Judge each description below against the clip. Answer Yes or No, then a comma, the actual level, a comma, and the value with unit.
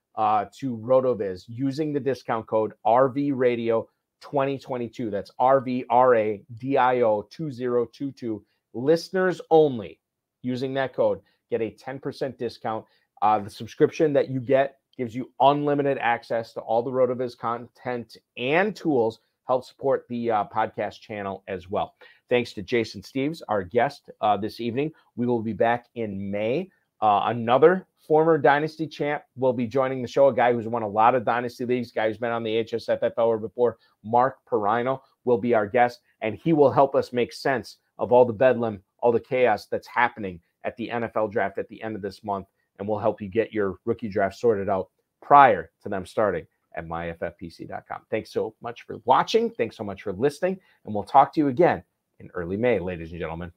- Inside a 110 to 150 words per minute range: No, average, 175 wpm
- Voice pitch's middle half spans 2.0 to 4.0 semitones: Yes, average, 3.6 semitones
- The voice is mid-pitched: No, low, 120 Hz